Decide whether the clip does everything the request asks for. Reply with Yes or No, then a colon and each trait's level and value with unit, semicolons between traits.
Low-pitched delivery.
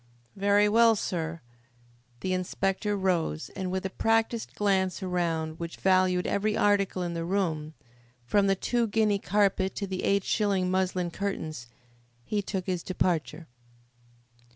No: high, 190 Hz